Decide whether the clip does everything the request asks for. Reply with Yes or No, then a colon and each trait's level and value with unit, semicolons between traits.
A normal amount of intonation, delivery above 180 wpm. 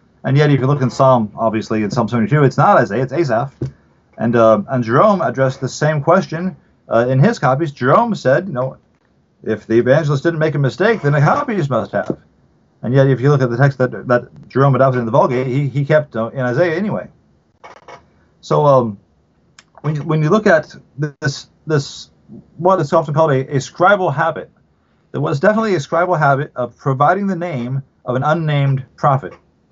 Yes: average, 3.7 semitones; average, 200 wpm